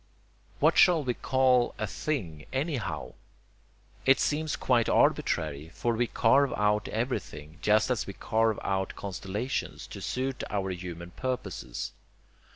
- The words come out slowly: Yes, slow, 130 wpm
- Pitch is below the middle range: Yes, low, 110 Hz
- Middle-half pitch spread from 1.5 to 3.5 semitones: No, wide, 5.4 semitones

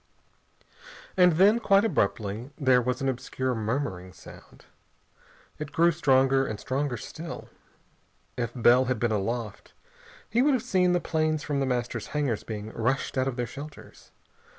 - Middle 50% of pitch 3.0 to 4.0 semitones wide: No, average, 4.9 semitones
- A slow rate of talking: No, average, 150 wpm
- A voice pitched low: Yes, low, 130 Hz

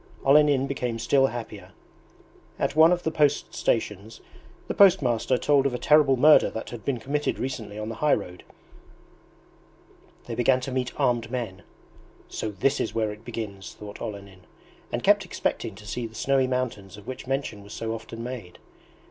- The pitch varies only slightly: No, average, 4.1 semitones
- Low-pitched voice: Yes, low, 120 Hz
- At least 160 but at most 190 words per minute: Yes, average, 175 wpm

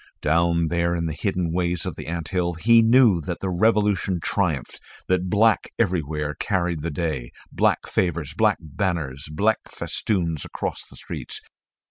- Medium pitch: No, very low, 85 Hz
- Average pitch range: Yes, average, 3.3 semitones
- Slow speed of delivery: No, average, 150 wpm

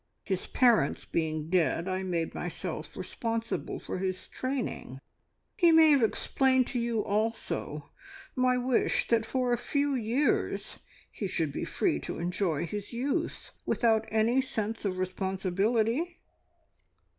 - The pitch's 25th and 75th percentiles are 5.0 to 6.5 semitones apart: Yes, wide, 5.4 semitones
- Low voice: No, high, 220 Hz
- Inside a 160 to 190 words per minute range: No, slow, 135 wpm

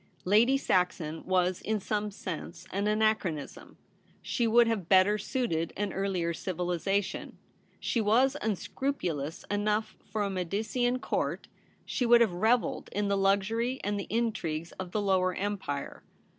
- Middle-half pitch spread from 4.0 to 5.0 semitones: No, average, 3.4 semitones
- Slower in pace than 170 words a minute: Yes, average, 140 wpm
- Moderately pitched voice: No, high, 200 Hz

